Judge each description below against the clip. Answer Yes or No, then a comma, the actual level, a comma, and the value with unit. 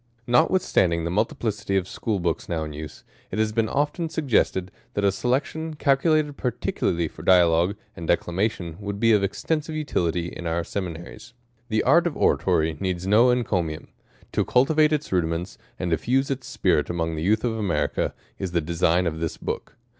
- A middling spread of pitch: No, wide, 6.6 semitones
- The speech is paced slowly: No, average, 170 wpm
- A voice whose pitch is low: Yes, low, 100 Hz